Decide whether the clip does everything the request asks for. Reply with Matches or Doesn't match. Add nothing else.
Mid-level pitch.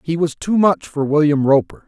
Matches